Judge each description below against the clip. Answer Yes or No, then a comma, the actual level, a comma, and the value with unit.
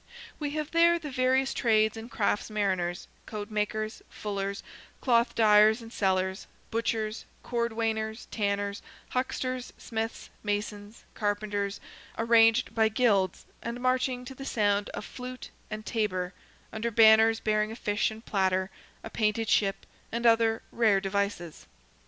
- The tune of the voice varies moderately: No, narrow, 2.2 semitones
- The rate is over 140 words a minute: No, slow, 135 wpm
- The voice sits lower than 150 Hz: No, high, 220 Hz